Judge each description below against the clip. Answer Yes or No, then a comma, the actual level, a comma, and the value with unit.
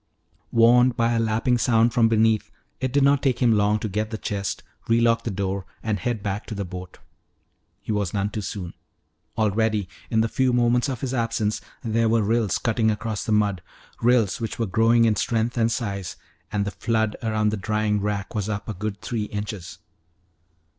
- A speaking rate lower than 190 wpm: No, average, 195 wpm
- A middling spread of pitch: No, narrow, 2.0 semitones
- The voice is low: Yes, low, 110 Hz